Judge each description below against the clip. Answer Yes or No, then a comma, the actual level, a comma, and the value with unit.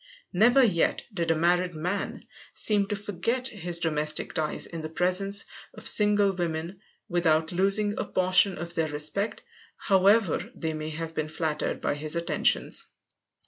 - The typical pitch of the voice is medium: Yes, medium, 175 Hz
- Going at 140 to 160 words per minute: Yes, average, 150 wpm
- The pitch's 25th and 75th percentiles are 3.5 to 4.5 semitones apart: Yes, average, 3.9 semitones